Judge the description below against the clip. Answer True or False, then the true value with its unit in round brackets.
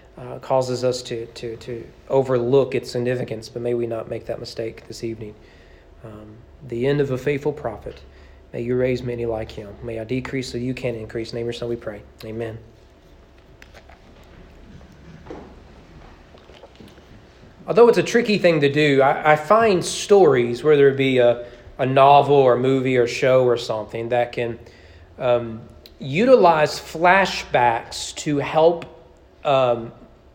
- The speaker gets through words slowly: False (155 wpm)